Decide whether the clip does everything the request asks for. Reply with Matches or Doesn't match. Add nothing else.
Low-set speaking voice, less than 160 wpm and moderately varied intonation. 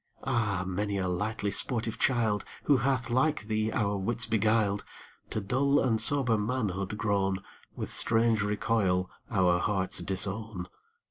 Matches